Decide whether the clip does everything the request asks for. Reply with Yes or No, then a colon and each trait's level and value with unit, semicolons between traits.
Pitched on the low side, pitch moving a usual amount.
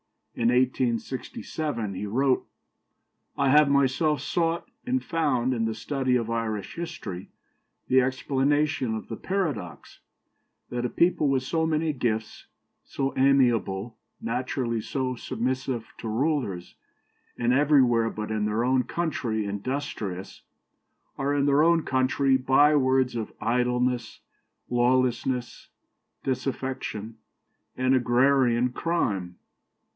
Yes: low, 130 Hz; average, 3.4 semitones